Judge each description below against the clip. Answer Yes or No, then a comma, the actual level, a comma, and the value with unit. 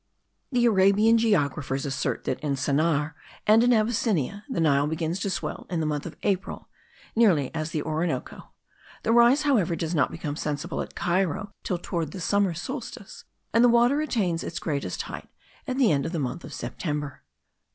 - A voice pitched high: No, medium, 175 Hz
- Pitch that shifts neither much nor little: No, wide, 6.6 semitones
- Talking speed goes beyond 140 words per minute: Yes, average, 180 wpm